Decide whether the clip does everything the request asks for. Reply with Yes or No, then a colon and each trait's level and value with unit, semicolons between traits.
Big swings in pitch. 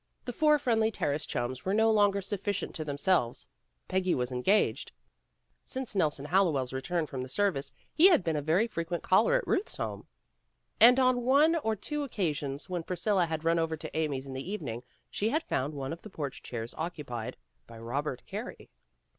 Yes: wide, 7.5 semitones